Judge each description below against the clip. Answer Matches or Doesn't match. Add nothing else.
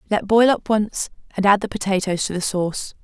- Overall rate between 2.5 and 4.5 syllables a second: Doesn't match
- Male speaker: Doesn't match